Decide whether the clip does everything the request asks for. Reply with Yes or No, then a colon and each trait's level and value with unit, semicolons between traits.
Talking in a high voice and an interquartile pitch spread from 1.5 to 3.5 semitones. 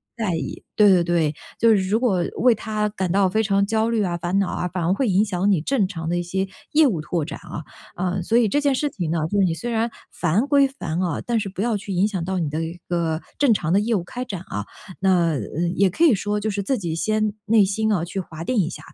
No: high, 195 Hz; average, 4.0 semitones